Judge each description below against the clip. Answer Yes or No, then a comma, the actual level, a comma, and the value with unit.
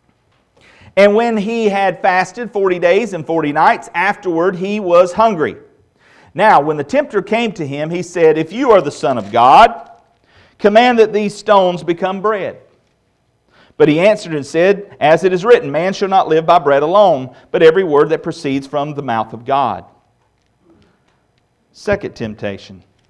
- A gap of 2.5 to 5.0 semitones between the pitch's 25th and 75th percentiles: No, wide, 5.6 semitones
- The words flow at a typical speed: Yes, average, 165 wpm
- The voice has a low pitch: No, medium, 180 Hz